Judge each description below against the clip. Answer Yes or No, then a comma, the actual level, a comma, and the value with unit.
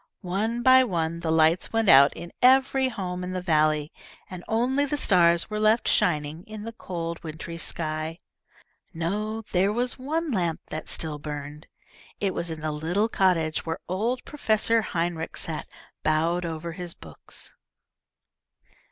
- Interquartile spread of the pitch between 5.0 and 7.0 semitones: Yes, average, 5.3 semitones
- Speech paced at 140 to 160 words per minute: Yes, average, 150 wpm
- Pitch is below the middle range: No, medium, 175 Hz